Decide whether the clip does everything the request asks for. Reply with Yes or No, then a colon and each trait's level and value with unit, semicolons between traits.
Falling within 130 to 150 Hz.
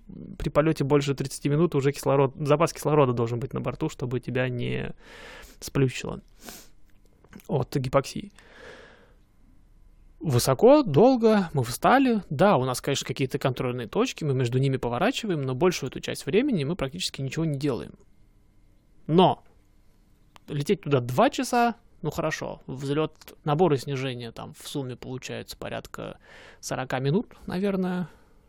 Yes: medium, 140 Hz